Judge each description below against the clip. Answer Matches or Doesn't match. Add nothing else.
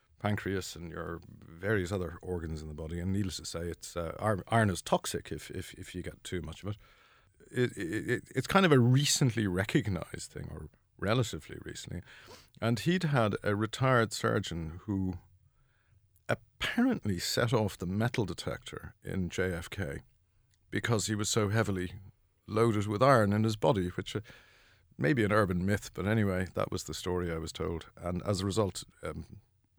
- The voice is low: Matches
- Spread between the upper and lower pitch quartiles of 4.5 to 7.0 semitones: Doesn't match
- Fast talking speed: Doesn't match